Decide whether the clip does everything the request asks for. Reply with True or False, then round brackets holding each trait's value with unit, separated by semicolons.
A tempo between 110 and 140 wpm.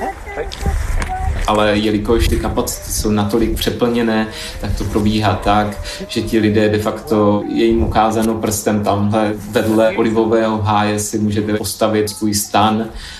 True (130 wpm)